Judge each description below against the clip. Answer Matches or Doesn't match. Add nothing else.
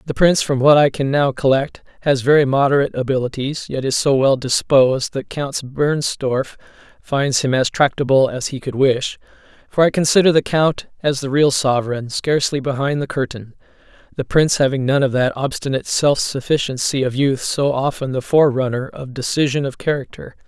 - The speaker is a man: Matches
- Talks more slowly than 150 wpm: Doesn't match